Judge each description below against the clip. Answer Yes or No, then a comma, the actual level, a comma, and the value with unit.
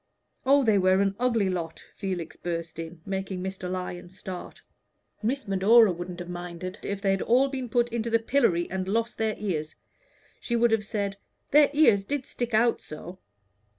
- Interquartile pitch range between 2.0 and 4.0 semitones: No, average, 4.4 semitones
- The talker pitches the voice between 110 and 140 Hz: No, high, 195 Hz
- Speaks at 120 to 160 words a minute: No, average, 180 wpm